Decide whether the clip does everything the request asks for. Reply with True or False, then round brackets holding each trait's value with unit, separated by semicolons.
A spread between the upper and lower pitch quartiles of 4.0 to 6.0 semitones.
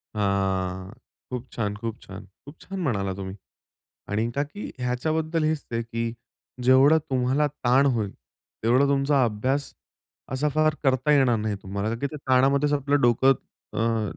True (4.7 semitones)